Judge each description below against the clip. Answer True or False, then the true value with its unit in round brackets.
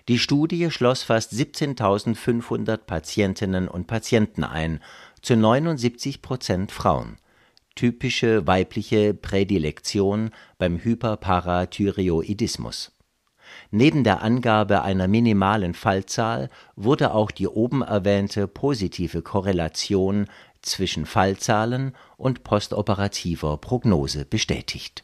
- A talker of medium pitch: False (105 Hz)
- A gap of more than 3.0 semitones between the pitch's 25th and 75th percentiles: True (4.1 semitones)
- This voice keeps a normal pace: False (85 wpm)